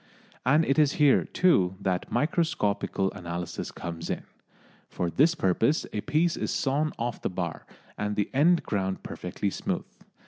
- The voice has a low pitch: Yes, low, 105 Hz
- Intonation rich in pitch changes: Yes, wide, 8.2 semitones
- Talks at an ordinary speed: Yes, average, 150 wpm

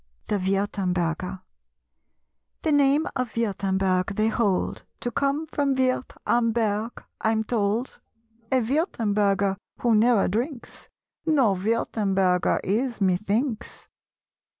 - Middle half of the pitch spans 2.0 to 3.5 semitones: No, average, 4.2 semitones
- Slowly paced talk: Yes, slow, 105 wpm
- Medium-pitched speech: No, high, 220 Hz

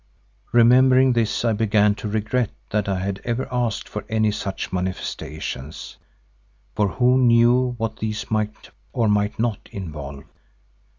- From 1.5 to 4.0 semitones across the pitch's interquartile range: Yes, average, 2.9 semitones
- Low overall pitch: Yes, low, 110 Hz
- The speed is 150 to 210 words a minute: No, slow, 135 wpm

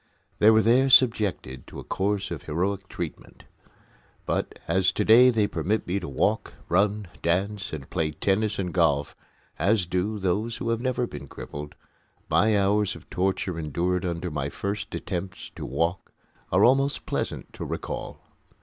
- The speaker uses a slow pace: No, average, 160 wpm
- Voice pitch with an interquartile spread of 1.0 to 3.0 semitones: No, average, 3.9 semitones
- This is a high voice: No, very low, 95 Hz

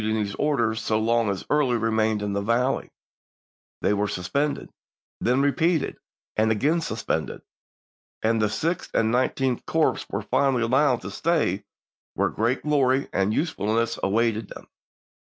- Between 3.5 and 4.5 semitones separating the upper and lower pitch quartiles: Yes, average, 4.1 semitones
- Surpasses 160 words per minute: No, average, 145 wpm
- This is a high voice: No, low, 115 Hz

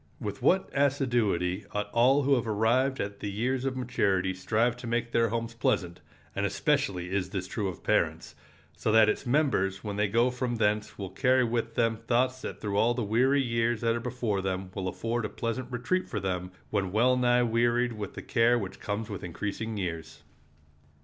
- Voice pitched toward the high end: No, low, 115 Hz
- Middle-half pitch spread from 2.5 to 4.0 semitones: Yes, average, 3.4 semitones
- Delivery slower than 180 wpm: No, average, 190 wpm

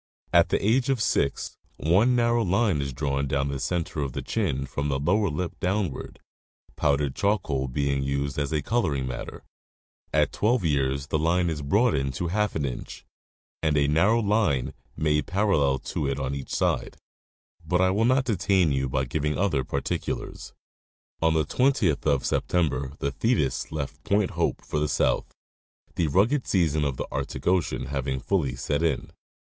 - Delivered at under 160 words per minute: No, average, 170 wpm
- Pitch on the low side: Yes, very low, 75 Hz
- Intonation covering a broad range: Yes, wide, 6.1 semitones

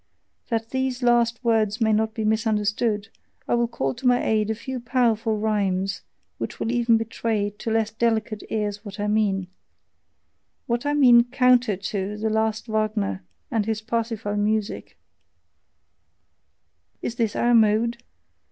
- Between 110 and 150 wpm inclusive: Yes, average, 145 wpm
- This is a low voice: No, high, 220 Hz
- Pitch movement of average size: No, narrow, 2.0 semitones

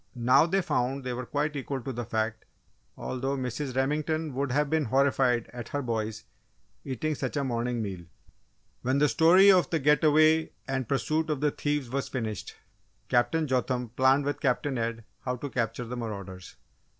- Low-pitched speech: Yes, low, 130 Hz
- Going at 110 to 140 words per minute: No, average, 175 wpm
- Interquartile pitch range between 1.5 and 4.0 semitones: Yes, average, 3.5 semitones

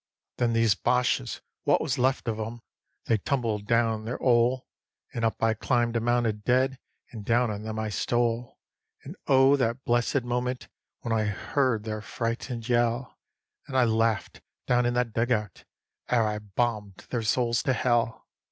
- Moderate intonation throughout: No, narrow, 1.8 semitones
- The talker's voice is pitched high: No, low, 120 Hz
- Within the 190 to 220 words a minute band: No, average, 170 wpm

